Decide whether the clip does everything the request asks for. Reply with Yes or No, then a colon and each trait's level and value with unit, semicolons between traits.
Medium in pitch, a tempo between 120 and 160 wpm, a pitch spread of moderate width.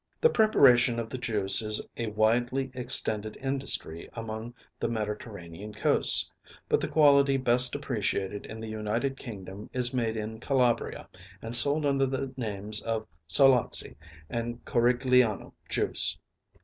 No: low, 115 Hz; slow, 135 wpm; average, 3.3 semitones